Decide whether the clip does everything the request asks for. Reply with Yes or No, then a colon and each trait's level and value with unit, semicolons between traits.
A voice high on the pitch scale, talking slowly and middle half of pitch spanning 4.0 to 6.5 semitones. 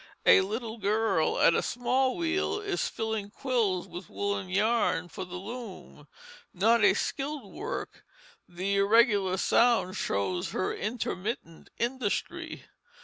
Yes: high, 210 Hz; slow, 125 wpm; average, 4.3 semitones